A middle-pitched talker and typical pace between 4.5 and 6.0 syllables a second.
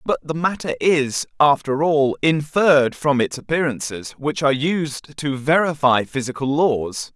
No: medium, 145 Hz; 4.3 syllables/s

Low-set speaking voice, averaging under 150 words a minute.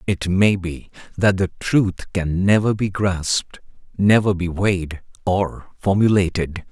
Yes: very low, 95 Hz; slow, 135 wpm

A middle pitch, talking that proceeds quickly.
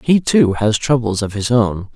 No: low, 115 Hz; fast, 215 wpm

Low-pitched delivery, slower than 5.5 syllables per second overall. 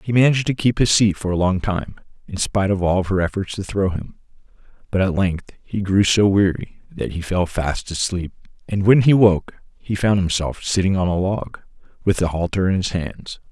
Yes: very low, 95 Hz; 5.0 syllables/s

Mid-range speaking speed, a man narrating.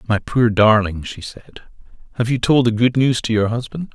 No: fast, 215 wpm; male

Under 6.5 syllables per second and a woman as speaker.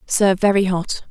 Yes: 5.5 syllables/s; female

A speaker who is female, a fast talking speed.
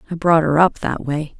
Yes: female; fast, 260 wpm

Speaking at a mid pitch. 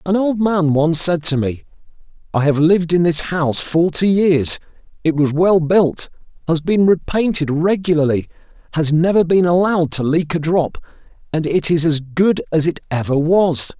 Yes: medium, 165 Hz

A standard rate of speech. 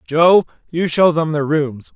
Yes: average, 185 wpm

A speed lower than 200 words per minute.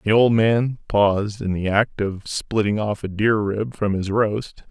No: fast, 205 wpm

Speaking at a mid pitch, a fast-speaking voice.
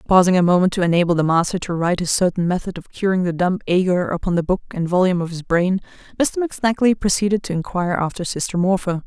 Yes: medium, 180 Hz; fast, 220 wpm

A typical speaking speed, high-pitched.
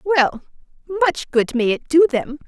Yes: average, 170 wpm; very high, 285 Hz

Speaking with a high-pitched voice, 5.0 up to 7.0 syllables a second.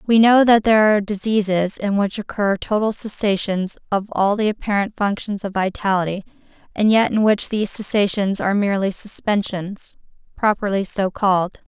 Yes: high, 200 Hz; 5.3 syllables/s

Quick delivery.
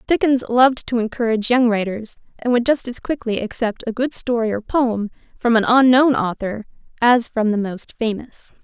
No: average, 180 wpm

